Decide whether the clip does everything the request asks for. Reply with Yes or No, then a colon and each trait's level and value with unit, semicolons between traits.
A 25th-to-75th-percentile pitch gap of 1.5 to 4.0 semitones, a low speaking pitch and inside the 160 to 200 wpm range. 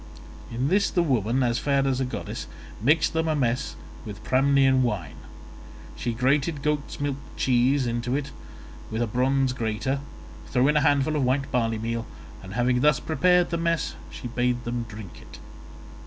Yes: average, 3.3 semitones; low, 130 Hz; average, 170 wpm